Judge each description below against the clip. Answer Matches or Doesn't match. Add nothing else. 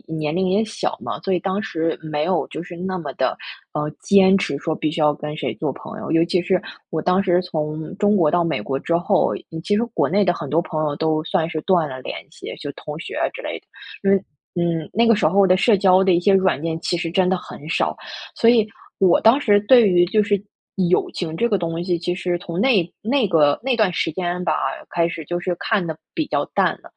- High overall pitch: Doesn't match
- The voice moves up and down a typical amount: Matches